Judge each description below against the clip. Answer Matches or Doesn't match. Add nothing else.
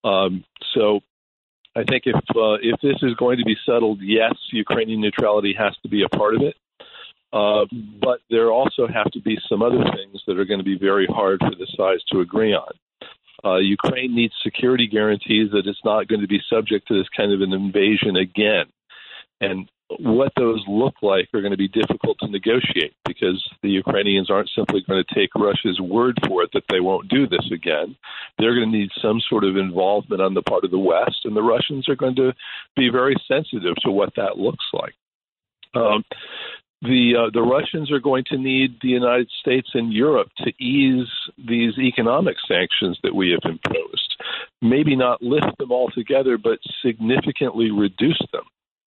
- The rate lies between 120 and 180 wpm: Doesn't match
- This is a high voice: Doesn't match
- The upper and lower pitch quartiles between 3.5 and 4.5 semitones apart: Matches